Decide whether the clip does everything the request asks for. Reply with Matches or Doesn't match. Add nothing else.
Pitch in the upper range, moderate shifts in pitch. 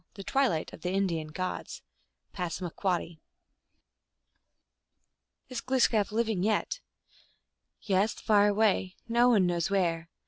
Matches